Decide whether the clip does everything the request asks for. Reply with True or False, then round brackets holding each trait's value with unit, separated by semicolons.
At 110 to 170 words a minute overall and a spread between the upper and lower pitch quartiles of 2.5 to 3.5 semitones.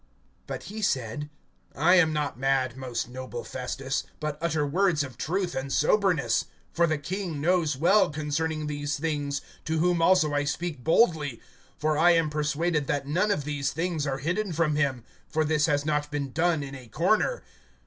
False (180 wpm; 3.1 semitones)